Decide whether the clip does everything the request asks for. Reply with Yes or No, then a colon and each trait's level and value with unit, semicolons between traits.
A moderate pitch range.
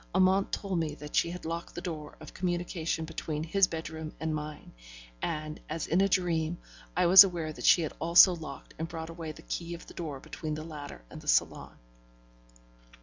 No: narrow, 2.2 semitones